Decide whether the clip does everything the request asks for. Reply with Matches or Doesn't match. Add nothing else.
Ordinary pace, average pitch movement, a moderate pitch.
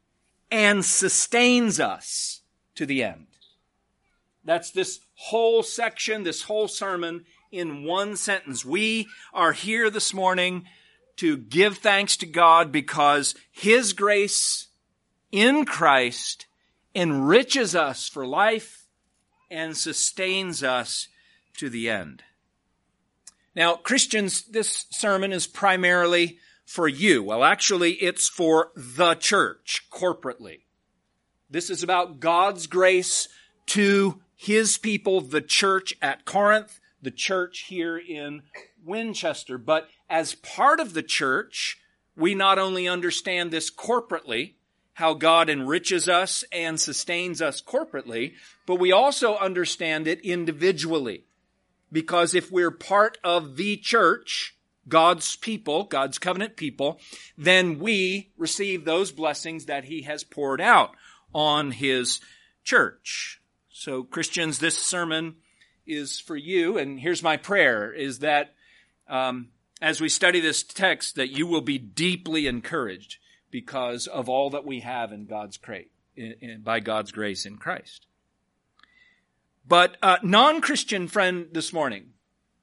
Doesn't match